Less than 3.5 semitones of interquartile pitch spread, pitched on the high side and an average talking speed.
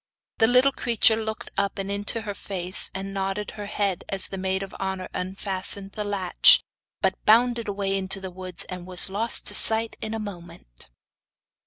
Yes: narrow, 2.4 semitones; high, 195 Hz; average, 180 wpm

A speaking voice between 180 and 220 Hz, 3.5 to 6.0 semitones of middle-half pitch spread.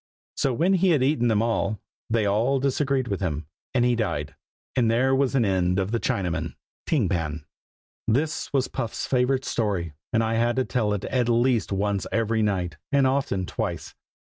No: low, 115 Hz; average, 4.9 semitones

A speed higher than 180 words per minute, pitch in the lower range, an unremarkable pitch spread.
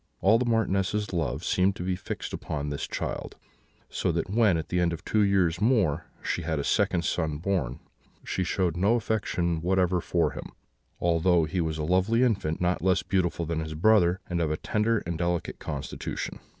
Yes: average, 190 wpm; very low, 90 Hz; average, 3.3 semitones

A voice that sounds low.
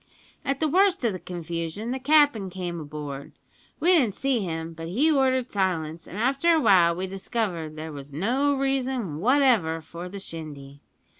No: high, 190 Hz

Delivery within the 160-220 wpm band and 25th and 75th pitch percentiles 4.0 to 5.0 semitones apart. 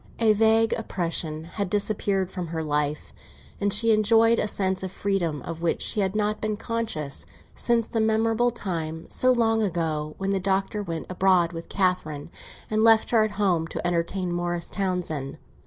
Yes: average, 170 wpm; average, 4.4 semitones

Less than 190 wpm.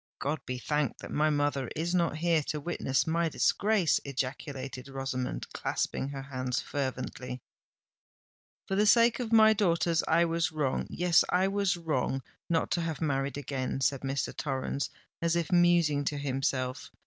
Yes: average, 155 wpm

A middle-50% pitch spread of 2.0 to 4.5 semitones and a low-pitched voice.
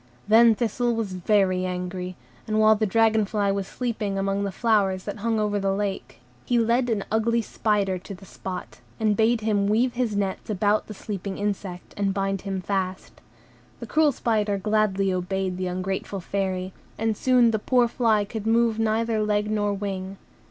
No: narrow, 2.4 semitones; high, 205 Hz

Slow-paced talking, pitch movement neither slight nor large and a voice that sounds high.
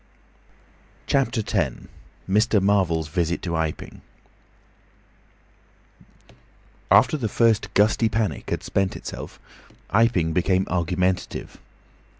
No: slow, 90 wpm; average, 4.1 semitones; very low, 95 Hz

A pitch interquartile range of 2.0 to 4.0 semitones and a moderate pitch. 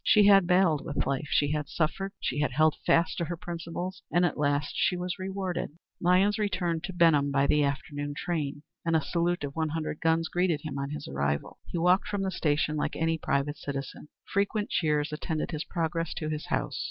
Yes: average, 3.3 semitones; medium, 160 Hz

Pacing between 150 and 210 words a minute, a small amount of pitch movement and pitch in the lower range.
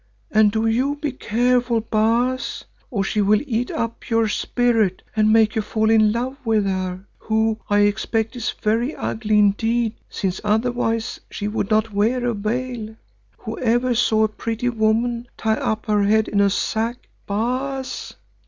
No: average, 160 wpm; narrow, 2.2 semitones; high, 220 Hz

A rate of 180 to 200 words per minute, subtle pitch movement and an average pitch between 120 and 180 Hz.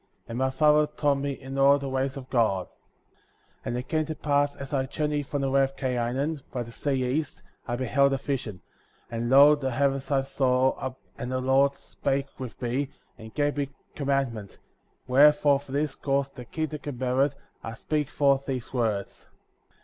Yes: average, 190 wpm; narrow, 1.9 semitones; low, 135 Hz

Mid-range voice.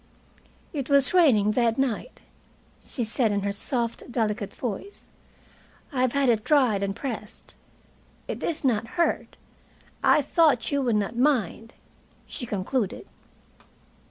No: high, 240 Hz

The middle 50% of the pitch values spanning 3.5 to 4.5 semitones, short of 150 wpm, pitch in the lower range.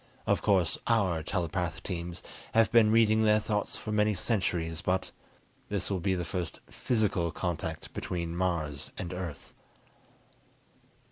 Yes: average, 3.8 semitones; slow, 135 wpm; very low, 90 Hz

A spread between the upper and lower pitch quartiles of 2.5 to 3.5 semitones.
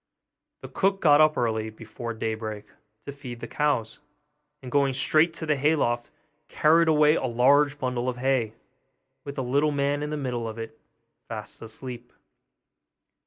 No: average, 3.9 semitones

